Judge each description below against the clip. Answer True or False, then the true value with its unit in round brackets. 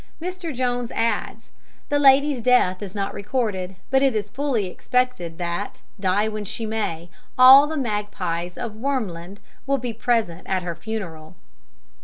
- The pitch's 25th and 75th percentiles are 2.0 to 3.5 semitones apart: False (5.5 semitones)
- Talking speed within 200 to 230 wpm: False (150 wpm)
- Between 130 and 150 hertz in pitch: False (220 Hz)